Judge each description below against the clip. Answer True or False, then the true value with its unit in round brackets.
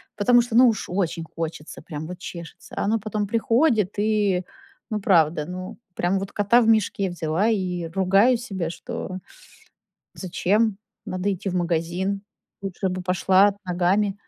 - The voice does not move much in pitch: False (3.1 semitones)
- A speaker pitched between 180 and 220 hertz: True (190 Hz)